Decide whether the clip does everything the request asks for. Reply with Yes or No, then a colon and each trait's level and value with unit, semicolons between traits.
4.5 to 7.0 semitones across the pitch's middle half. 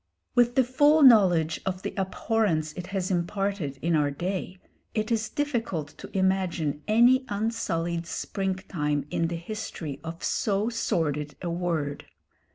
Yes: average, 4.8 semitones